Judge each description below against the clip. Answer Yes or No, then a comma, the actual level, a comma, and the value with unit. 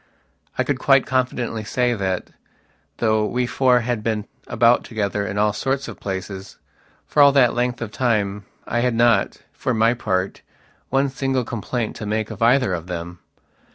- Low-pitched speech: Yes, low, 115 Hz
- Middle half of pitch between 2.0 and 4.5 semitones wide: Yes, average, 3.3 semitones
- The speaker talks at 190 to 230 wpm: No, average, 170 wpm